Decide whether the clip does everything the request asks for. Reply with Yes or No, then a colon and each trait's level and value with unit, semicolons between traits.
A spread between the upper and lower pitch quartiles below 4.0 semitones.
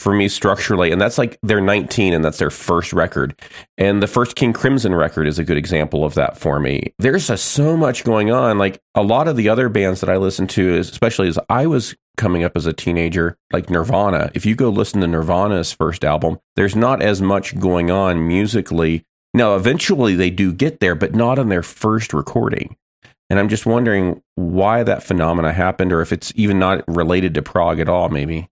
No: average, 4.4 semitones